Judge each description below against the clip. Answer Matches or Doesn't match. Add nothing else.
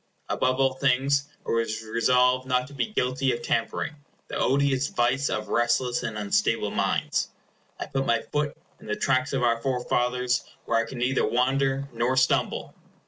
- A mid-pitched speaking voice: Doesn't match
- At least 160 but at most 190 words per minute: Matches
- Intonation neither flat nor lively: Doesn't match